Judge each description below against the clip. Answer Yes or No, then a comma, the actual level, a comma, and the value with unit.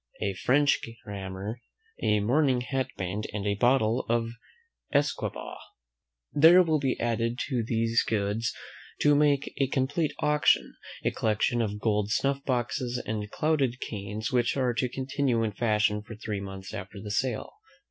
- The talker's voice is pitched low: Yes, low, 115 Hz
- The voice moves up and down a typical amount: Yes, average, 4.2 semitones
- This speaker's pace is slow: No, average, 155 wpm